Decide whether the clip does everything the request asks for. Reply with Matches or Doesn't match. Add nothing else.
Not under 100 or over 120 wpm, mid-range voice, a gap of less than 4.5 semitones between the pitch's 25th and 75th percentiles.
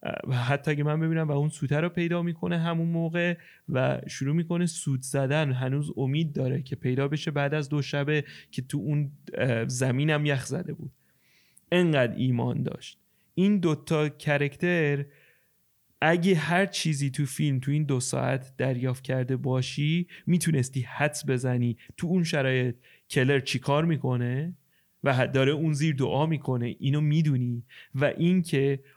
Doesn't match